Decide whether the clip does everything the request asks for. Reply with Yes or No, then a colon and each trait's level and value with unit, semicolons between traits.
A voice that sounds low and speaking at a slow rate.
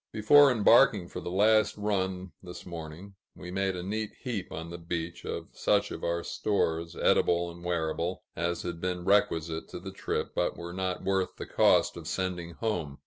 No: very low, 90 Hz; average, 185 wpm